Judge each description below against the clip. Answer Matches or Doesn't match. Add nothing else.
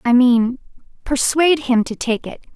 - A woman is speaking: Matches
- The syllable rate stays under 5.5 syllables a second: Matches